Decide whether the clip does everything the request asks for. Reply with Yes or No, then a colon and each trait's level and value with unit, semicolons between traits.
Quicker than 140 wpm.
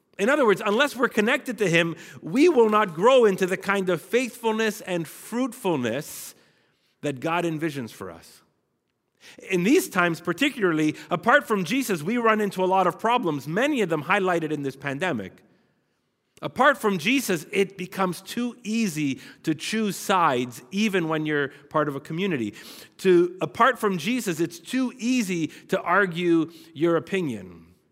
Yes: average, 155 wpm